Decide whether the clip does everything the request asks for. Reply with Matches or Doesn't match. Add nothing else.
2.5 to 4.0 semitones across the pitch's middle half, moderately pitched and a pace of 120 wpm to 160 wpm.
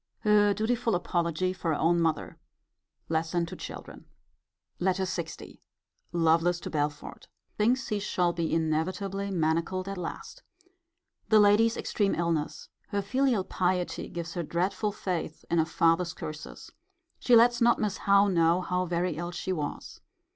Matches